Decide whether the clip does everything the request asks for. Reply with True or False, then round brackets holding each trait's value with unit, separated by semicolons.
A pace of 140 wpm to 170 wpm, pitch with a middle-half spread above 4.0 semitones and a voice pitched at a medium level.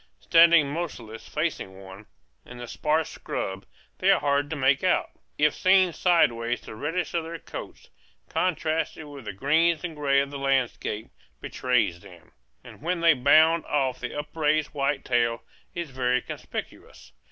True (155 wpm; 4.8 semitones; 145 Hz)